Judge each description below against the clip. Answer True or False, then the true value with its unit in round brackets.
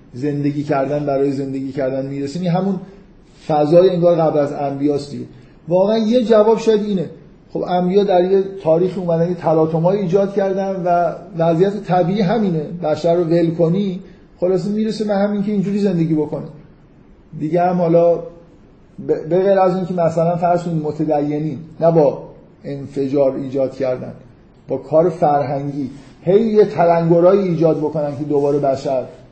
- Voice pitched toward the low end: False (170 Hz)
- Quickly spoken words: False (145 wpm)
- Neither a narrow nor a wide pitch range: True (4.1 semitones)